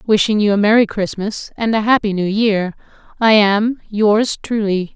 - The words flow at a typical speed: Yes, average, 170 wpm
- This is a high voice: Yes, high, 210 Hz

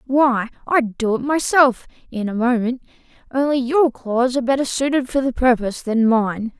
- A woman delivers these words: No, male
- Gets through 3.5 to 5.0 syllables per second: Yes, 4.9 syllables/s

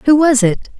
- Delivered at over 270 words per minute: No, fast, 225 wpm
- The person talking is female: Yes, female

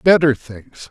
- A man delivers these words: Yes, male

